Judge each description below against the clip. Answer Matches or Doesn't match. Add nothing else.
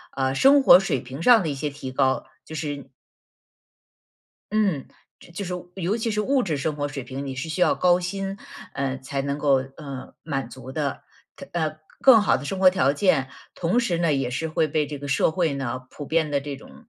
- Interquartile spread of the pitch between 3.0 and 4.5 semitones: Doesn't match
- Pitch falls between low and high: Matches